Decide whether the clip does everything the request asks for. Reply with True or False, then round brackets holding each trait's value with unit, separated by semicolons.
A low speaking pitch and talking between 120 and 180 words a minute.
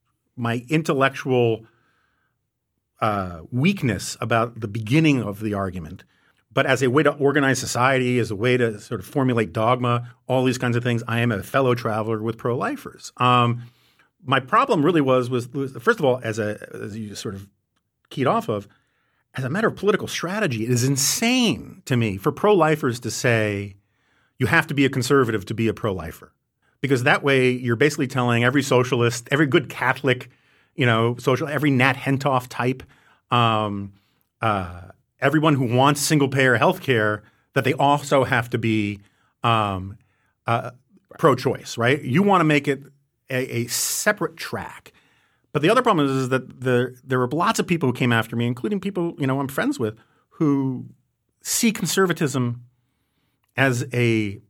True (125 Hz; 175 wpm)